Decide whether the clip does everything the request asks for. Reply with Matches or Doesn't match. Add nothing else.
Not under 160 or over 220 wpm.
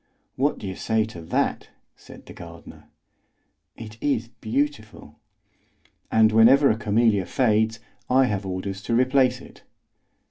Doesn't match